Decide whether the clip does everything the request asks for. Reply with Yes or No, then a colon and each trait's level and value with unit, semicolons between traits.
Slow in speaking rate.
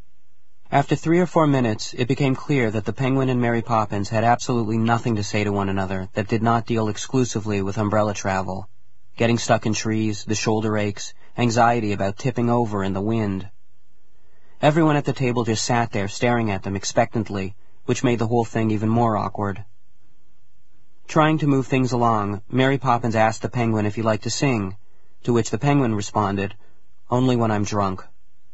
No: average, 185 wpm